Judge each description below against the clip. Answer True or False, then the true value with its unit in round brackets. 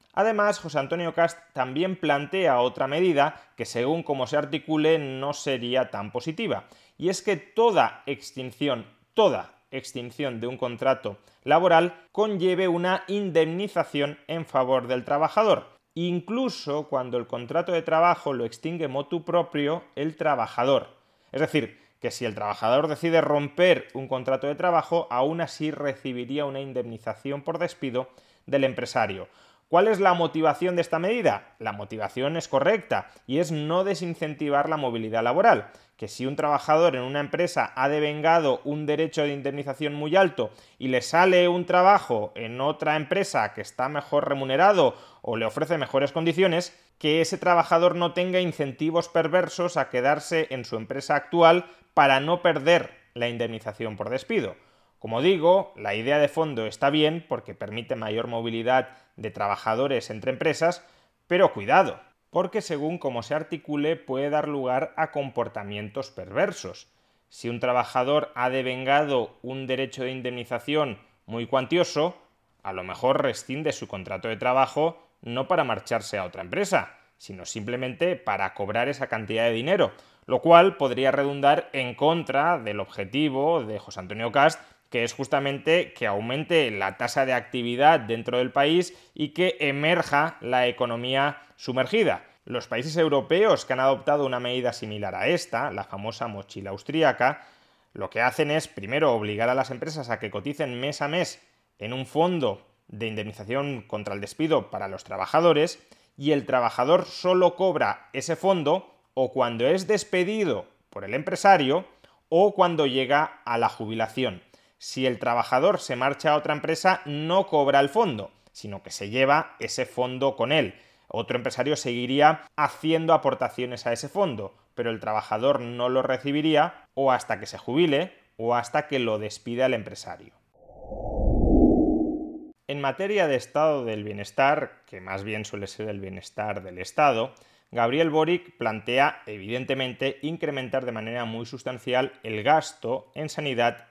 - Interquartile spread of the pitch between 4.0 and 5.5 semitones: True (4.9 semitones)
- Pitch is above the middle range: False (140 Hz)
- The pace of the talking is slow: False (150 wpm)